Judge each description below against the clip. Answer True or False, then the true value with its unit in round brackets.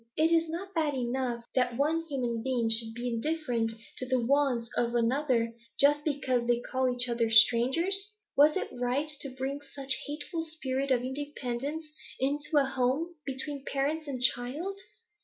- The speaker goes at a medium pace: True (165 wpm)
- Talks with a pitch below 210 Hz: False (265 Hz)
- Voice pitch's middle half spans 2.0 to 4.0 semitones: True (3.4 semitones)